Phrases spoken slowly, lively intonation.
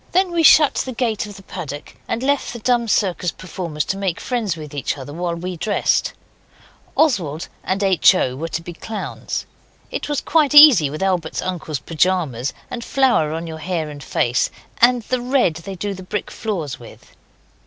No: average, 185 wpm; wide, 6.9 semitones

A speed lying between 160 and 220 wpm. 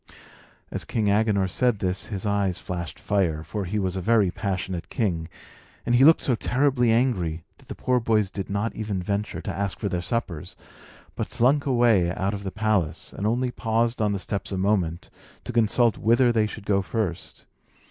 Yes: average, 190 wpm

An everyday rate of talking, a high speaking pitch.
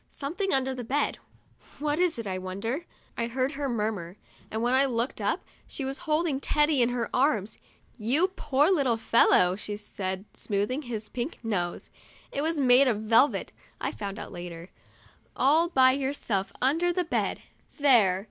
Yes: average, 170 wpm; very high, 255 Hz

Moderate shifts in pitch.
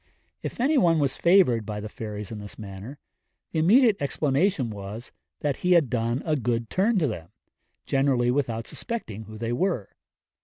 No: wide, 7.3 semitones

